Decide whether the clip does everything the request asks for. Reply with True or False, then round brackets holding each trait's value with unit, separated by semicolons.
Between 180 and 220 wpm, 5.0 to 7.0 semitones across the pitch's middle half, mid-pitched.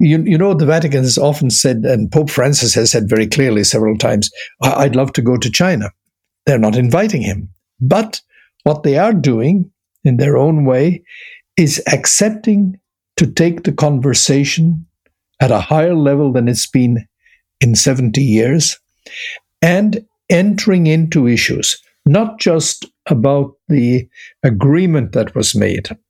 False (145 wpm; 5.6 semitones; 145 Hz)